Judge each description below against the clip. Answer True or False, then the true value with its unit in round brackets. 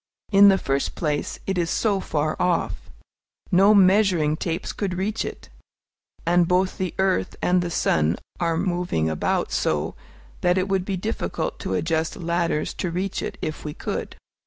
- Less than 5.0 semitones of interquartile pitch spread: True (2.9 semitones)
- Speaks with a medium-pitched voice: True (180 Hz)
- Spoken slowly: False (165 wpm)